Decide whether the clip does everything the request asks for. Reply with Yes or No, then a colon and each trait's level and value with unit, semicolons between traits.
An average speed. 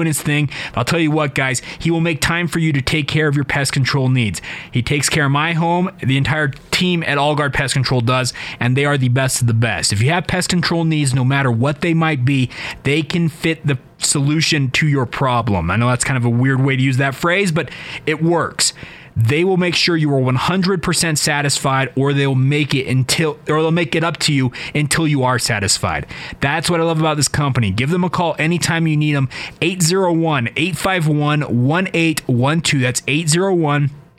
No: fast, 215 wpm